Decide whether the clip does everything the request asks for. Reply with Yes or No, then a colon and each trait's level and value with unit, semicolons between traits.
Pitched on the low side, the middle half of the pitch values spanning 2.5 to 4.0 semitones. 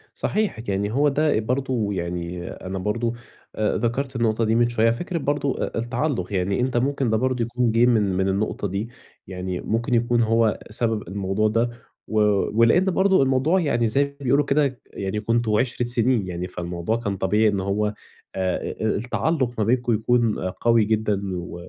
Yes: low, 115 Hz; average, 3.7 semitones